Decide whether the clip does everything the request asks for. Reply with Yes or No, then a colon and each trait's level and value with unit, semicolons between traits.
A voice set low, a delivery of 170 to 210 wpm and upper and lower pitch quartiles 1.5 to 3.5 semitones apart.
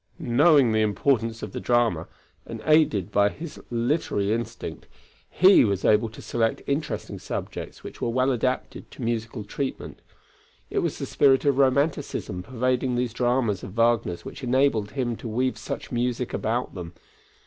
No: low, 120 Hz; average, 160 wpm; average, 3.2 semitones